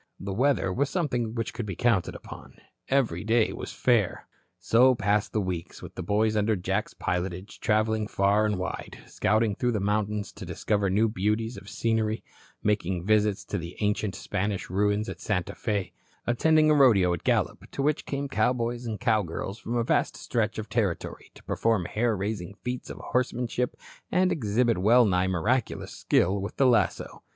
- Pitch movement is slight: No, average, 3.3 semitones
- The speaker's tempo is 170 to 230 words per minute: Yes, average, 175 wpm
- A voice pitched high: No, low, 110 Hz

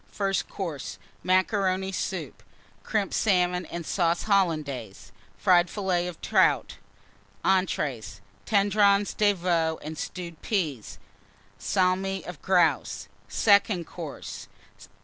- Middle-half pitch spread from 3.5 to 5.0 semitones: No, average, 3.0 semitones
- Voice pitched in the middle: Yes, medium, 180 Hz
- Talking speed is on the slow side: Yes, slow, 100 wpm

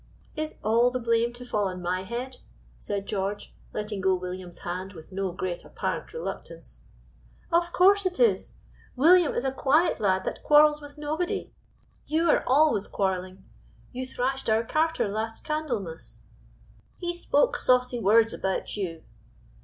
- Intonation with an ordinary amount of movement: No, wide, 7.9 semitones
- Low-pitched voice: No, high, 235 Hz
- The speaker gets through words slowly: No, average, 150 wpm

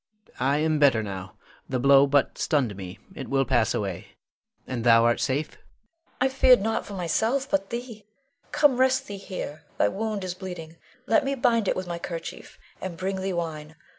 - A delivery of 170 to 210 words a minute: Yes, average, 190 wpm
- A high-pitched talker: No, medium, 170 Hz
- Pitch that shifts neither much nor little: No, wide, 8.1 semitones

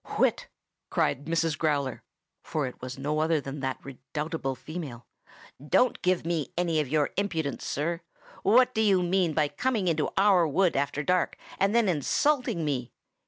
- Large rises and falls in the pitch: No, average, 4.5 semitones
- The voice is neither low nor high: Yes, medium, 160 Hz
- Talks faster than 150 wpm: Yes, average, 165 wpm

